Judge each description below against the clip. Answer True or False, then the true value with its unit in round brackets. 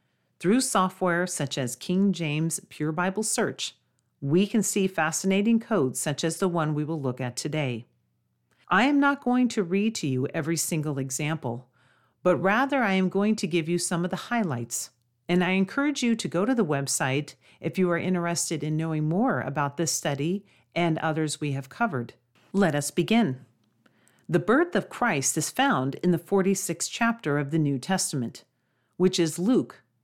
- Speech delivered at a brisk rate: False (180 wpm)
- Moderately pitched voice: True (170 Hz)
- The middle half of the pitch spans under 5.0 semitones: False (5.3 semitones)